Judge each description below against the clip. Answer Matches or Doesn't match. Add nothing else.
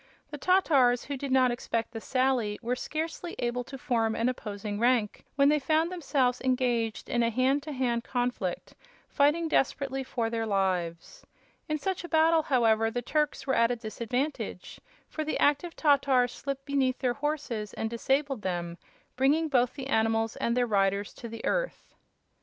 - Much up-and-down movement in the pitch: Doesn't match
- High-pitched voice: Matches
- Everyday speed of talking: Matches